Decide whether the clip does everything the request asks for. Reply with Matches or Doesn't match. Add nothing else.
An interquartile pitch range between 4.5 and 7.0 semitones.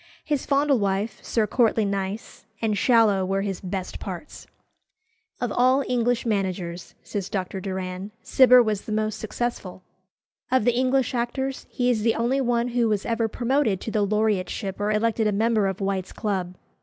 Doesn't match